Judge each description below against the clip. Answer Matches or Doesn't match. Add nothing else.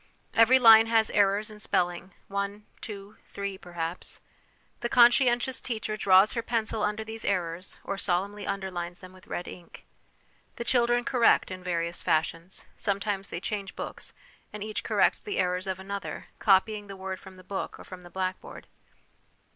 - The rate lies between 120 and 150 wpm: Doesn't match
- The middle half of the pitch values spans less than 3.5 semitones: Matches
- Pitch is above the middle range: Matches